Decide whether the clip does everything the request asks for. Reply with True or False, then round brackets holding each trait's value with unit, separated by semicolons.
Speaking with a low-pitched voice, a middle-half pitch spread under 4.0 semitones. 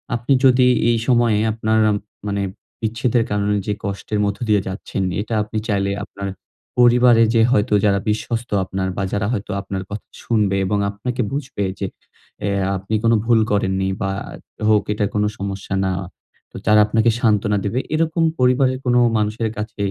True (105 Hz; 2.9 semitones)